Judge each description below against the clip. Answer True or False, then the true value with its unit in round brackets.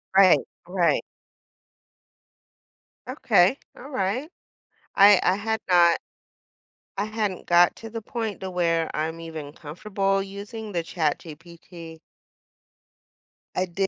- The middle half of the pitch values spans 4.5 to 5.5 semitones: False (3.6 semitones)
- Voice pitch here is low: False (185 Hz)